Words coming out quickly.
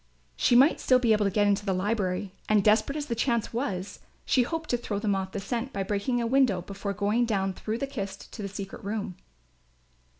Yes: fast, 225 wpm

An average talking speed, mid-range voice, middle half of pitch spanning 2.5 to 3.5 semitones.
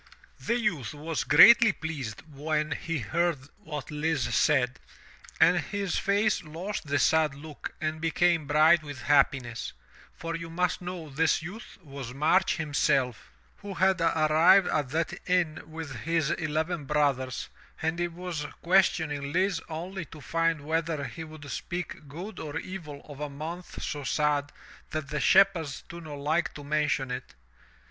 Yes: average, 155 wpm; medium, 155 Hz; average, 2.8 semitones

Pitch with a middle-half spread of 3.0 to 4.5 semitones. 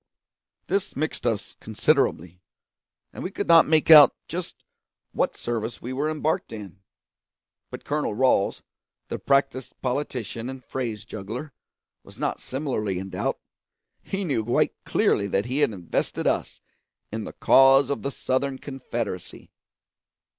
No: average, 4.9 semitones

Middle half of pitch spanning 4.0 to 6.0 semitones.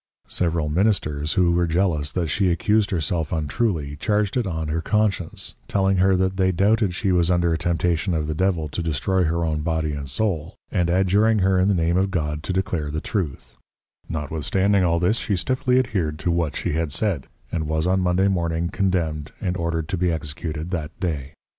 No: average, 3.3 semitones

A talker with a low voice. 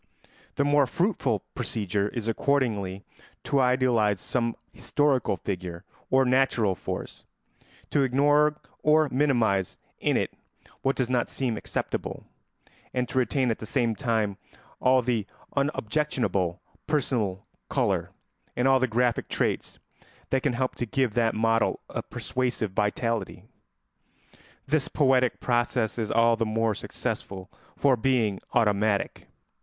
Yes: low, 120 Hz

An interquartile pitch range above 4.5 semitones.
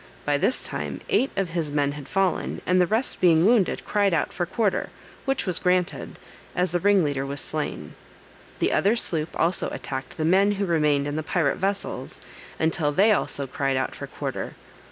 Yes: average, 5.0 semitones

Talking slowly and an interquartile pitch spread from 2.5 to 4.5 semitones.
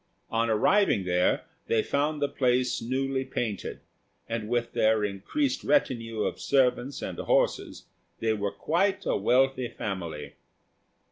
Yes: slow, 130 wpm; average, 4.1 semitones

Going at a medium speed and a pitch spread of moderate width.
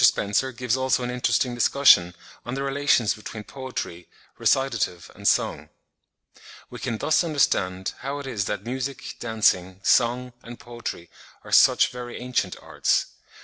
Yes: average, 145 wpm; average, 3.8 semitones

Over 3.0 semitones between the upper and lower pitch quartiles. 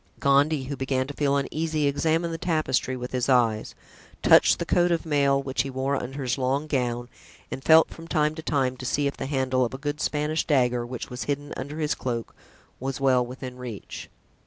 No: average, 2.7 semitones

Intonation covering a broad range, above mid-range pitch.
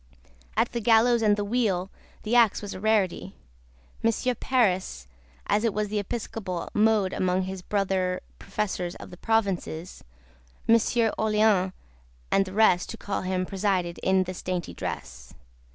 No: average, 3.1 semitones; high, 200 Hz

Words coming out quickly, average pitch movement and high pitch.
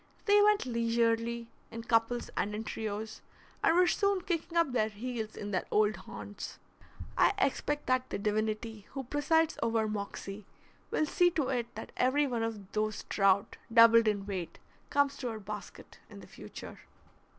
No: average, 165 wpm; average, 4.4 semitones; high, 230 Hz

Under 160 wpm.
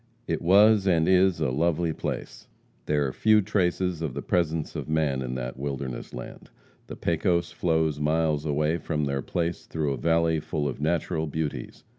No: average, 175 wpm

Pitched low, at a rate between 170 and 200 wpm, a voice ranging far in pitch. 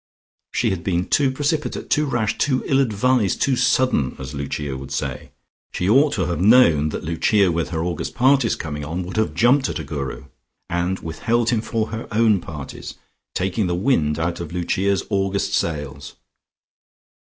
Yes: very low, 95 Hz; average, 175 wpm; wide, 6.7 semitones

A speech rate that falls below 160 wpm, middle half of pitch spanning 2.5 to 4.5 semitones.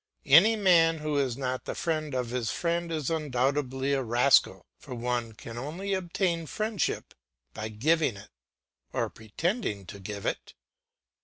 No: average, 150 wpm; wide, 5.5 semitones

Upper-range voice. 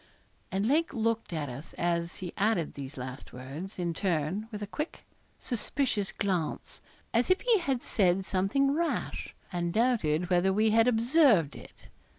Yes: high, 195 Hz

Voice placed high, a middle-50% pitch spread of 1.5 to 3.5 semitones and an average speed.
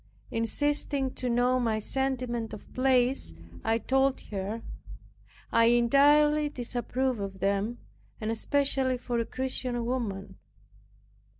No: high, 245 Hz; average, 2.8 semitones; slow, 110 wpm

